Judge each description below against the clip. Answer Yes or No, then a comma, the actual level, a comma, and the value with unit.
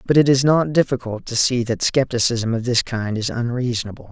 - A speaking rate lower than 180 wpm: No, fast, 205 wpm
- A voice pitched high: No, low, 125 Hz